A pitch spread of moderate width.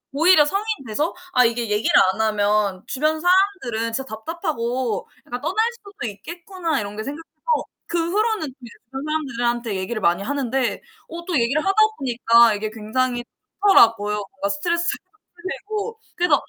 No: wide, 7.3 semitones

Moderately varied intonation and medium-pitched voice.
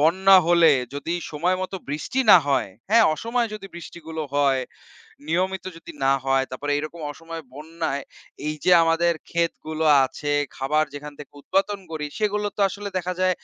Yes: average, 3.9 semitones; medium, 165 Hz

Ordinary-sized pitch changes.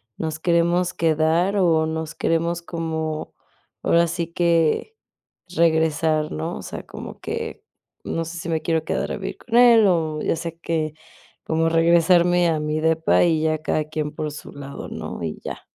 No: narrow, 1.4 semitones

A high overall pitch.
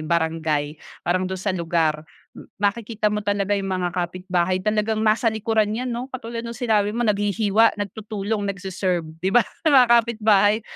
Yes: high, 205 Hz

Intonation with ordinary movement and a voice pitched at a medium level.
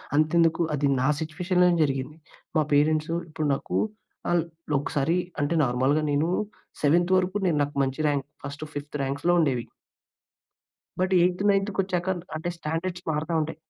Yes: average, 3.3 semitones; medium, 155 Hz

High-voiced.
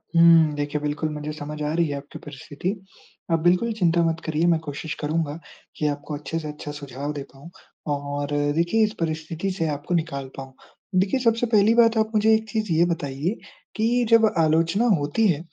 No: medium, 160 Hz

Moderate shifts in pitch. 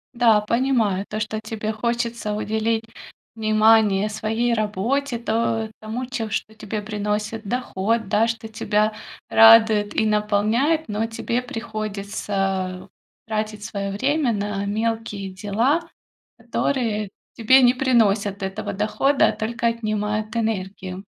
No: narrow, 1.8 semitones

